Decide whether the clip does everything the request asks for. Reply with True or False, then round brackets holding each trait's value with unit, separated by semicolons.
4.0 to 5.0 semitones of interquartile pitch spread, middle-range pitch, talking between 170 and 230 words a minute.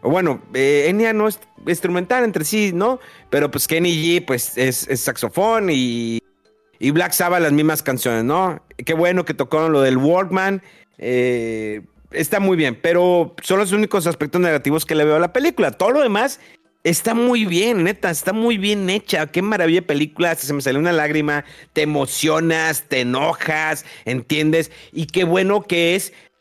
True (4.4 semitones; 165 Hz; 180 wpm)